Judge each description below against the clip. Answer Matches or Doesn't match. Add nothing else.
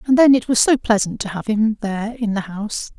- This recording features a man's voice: Doesn't match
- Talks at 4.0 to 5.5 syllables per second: Doesn't match